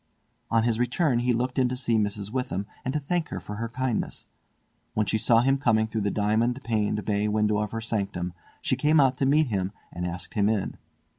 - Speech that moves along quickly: Yes, fast, 220 wpm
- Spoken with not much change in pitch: No, average, 3.4 semitones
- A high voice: No, low, 115 Hz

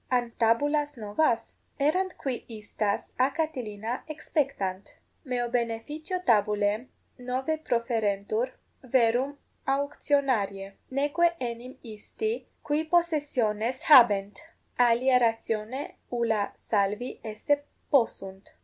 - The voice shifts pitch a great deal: No, average, 4.8 semitones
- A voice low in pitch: No, high, 245 Hz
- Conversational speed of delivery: No, slow, 90 wpm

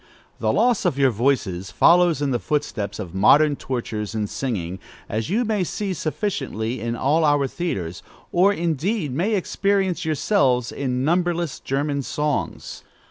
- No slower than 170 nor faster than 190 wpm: No, average, 145 wpm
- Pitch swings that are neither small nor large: No, wide, 7.0 semitones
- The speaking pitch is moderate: Yes, medium, 145 Hz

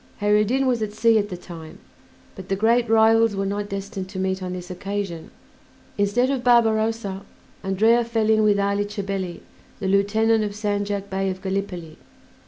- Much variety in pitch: No, narrow, 2.4 semitones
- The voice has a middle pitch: No, high, 205 Hz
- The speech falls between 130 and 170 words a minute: No, average, 180 wpm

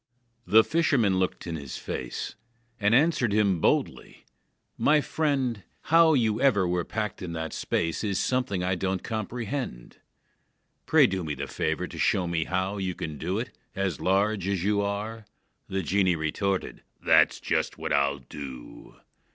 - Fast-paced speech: No, average, 160 wpm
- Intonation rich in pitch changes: No, average, 4.3 semitones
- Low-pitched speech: Yes, very low, 95 Hz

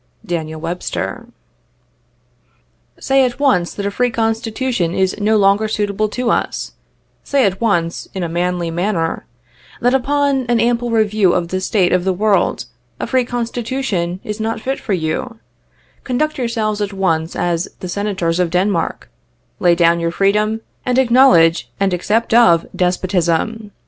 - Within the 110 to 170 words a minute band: Yes, average, 155 wpm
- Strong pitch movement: No, average, 4.8 semitones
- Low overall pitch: No, high, 205 Hz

